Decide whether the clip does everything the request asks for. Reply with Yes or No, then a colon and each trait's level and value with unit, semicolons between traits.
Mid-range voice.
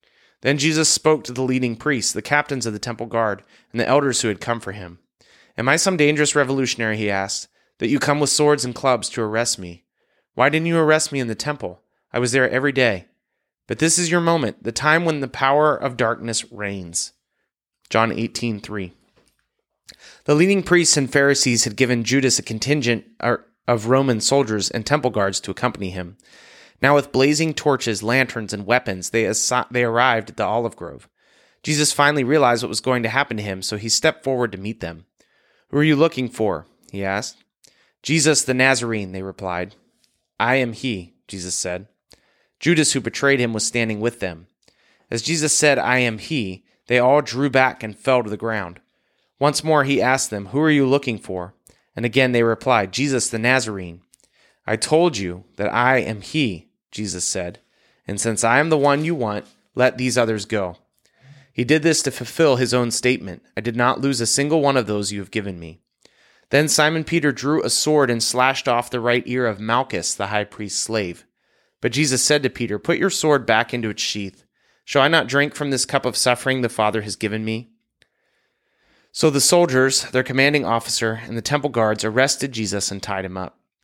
No: low, 125 Hz